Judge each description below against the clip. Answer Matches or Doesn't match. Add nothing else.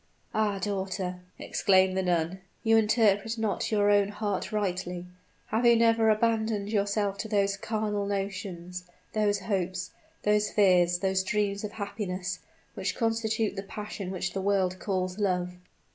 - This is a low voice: Doesn't match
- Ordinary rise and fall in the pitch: Doesn't match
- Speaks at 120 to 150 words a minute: Matches